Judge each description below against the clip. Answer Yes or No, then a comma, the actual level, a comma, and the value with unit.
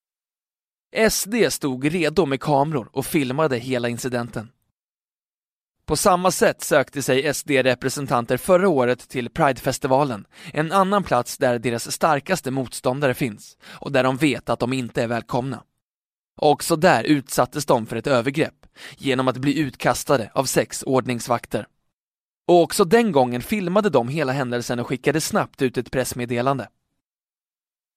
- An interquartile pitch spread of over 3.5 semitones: Yes, average, 4.1 semitones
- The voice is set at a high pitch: No, low, 135 Hz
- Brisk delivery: No, average, 135 wpm